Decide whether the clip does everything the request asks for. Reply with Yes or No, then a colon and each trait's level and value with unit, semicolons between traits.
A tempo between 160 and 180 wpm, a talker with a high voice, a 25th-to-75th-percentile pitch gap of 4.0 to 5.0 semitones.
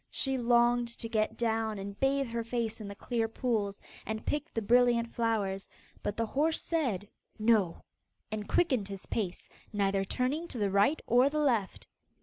No: average, 170 wpm; high, 230 Hz; average, 3.3 semitones